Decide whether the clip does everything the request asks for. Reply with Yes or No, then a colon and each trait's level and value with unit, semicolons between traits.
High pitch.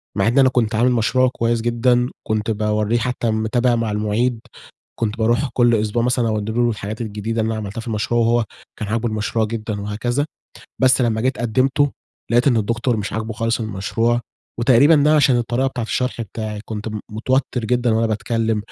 No: low, 115 Hz